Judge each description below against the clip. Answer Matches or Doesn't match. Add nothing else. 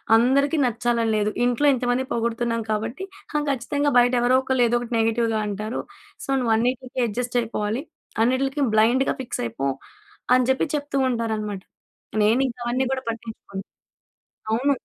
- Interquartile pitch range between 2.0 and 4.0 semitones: Matches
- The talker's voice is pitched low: Doesn't match